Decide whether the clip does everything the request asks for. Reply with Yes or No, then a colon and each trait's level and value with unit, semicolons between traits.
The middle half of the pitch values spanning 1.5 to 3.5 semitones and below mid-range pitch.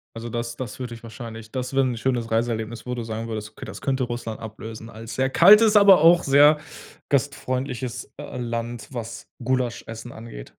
Yes: narrow, 2.5 semitones; low, 120 Hz